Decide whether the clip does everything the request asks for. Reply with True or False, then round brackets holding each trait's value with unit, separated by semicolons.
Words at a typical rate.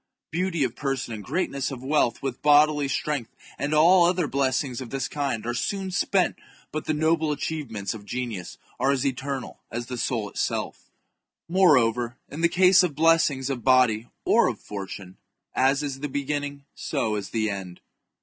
True (170 wpm)